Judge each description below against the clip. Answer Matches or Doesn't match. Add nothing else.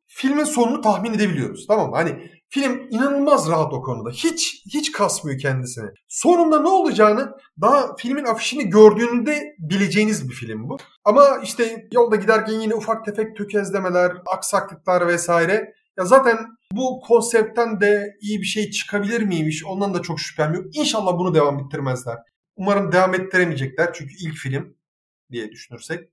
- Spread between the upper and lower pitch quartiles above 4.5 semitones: Matches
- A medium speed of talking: Doesn't match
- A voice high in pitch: Matches